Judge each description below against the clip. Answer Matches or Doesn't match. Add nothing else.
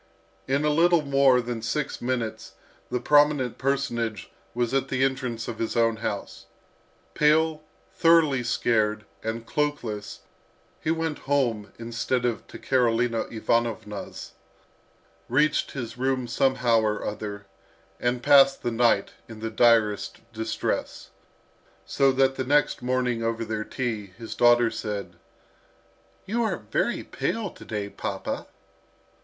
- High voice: Doesn't match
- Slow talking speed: Matches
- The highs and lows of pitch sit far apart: Doesn't match